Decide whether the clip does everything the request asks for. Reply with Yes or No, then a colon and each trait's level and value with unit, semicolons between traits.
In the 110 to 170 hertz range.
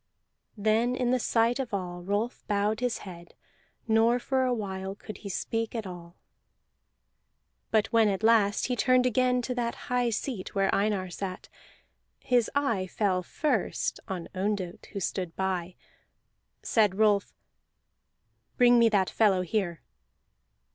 No: high, 215 Hz